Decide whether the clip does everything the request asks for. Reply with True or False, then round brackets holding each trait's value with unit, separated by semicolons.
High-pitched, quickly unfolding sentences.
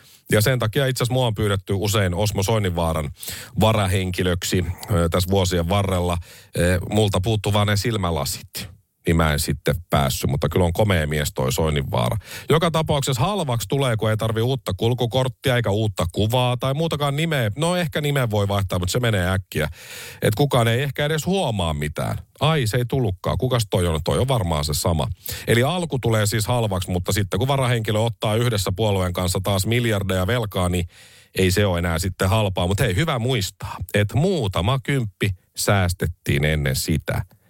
False (105 Hz; 170 wpm)